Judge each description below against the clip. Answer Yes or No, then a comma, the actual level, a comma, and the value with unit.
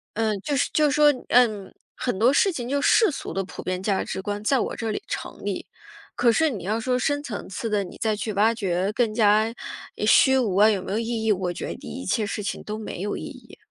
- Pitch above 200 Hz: Yes, high, 220 Hz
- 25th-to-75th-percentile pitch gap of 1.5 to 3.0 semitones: No, average, 3.5 semitones